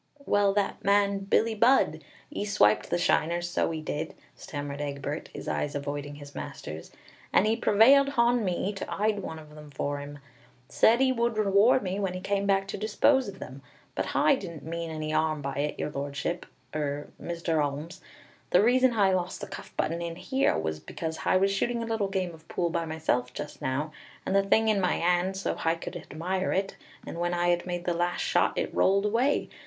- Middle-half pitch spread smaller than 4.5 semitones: No, average, 4.9 semitones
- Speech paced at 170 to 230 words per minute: Yes, fast, 205 wpm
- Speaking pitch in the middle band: Yes, medium, 175 Hz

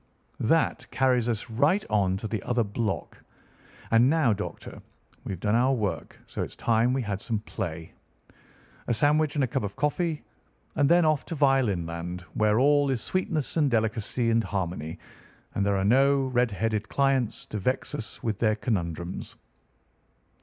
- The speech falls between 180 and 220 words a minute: No, average, 165 wpm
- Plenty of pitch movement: No, average, 5.0 semitones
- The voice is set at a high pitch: No, low, 115 Hz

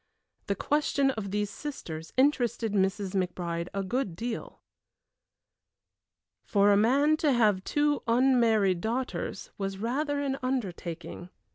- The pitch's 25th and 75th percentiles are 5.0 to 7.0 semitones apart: Yes, wide, 5.5 semitones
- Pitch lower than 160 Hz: No, high, 220 Hz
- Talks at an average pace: No, slow, 120 wpm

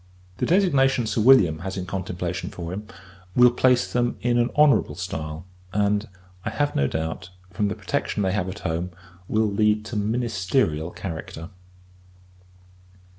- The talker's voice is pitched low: Yes, low, 100 Hz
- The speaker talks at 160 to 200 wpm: No, average, 150 wpm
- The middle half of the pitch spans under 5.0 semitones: No, average, 5.3 semitones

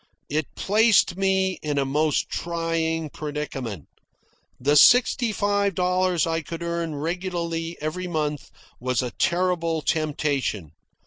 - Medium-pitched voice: Yes, medium, 165 Hz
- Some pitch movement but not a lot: Yes, average, 3.5 semitones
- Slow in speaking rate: Yes, slow, 120 wpm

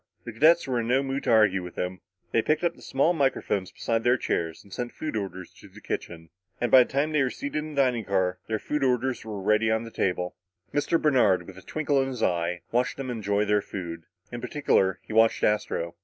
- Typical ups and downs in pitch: No, wide, 5.8 semitones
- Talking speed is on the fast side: Yes, fast, 230 wpm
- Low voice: Yes, low, 115 Hz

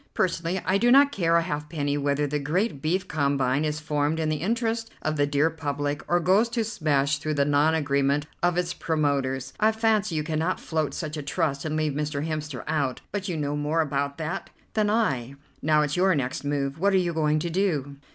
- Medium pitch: Yes, medium, 155 Hz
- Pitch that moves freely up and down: No, average, 3.5 semitones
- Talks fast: Yes, fast, 210 wpm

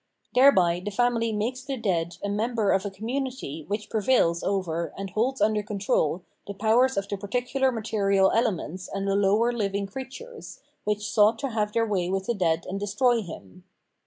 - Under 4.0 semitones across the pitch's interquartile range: Yes, average, 3.4 semitones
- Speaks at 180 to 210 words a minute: Yes, average, 185 wpm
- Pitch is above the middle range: Yes, high, 210 Hz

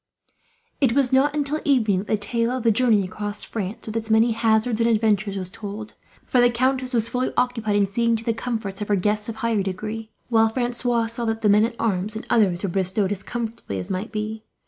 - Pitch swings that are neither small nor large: No, narrow, 2.3 semitones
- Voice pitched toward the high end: Yes, high, 220 Hz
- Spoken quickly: Yes, fast, 225 wpm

